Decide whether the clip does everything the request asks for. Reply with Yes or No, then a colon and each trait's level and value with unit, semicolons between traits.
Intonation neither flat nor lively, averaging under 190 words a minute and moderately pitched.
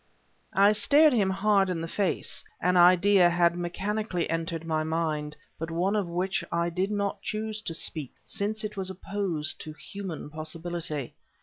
Yes: average, 3.5 semitones; average, 165 wpm; medium, 180 Hz